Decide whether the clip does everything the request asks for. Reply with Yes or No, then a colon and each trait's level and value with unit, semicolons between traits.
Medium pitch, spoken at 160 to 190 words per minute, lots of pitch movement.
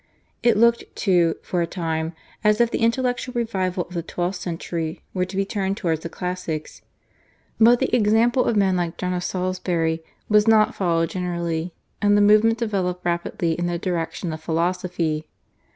No: medium, 180 Hz; average, 170 wpm; average, 3.8 semitones